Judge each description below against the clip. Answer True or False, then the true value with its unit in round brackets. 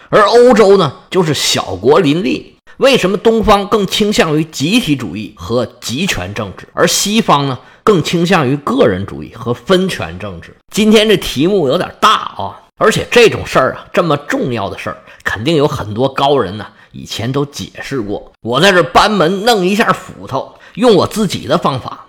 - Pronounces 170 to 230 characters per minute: False (270 characters per minute)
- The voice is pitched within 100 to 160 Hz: False (175 Hz)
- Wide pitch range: True (8.6 semitones)